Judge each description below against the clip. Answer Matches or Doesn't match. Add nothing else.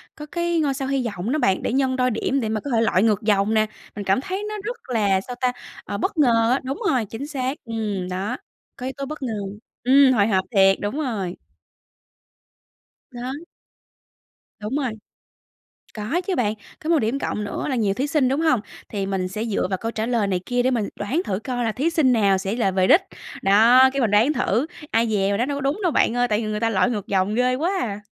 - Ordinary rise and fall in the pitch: Matches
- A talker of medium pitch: Doesn't match